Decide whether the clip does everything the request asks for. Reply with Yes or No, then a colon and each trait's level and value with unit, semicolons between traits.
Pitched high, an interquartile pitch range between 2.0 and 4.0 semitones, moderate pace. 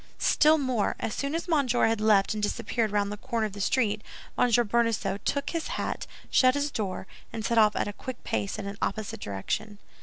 No: high, 220 Hz; average, 3.7 semitones; fast, 210 wpm